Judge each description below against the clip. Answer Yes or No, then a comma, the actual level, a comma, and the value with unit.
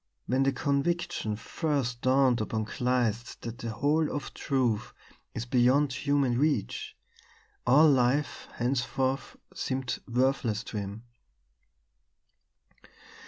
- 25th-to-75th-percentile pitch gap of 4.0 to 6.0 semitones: No, average, 2.8 semitones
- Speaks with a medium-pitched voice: No, low, 130 Hz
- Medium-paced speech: No, slow, 105 wpm